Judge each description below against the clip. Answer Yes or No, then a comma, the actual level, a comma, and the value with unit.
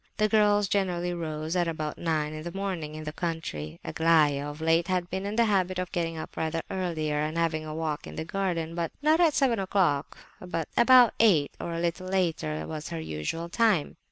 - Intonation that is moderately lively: Yes, average, 3.4 semitones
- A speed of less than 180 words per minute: No, fast, 205 wpm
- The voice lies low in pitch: No, medium, 165 Hz